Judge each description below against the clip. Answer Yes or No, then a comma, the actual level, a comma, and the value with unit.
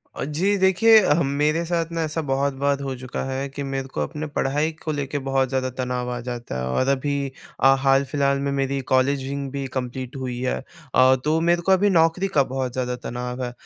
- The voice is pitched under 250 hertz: Yes, medium, 140 Hz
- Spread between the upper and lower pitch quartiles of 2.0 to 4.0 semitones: Yes, average, 2.8 semitones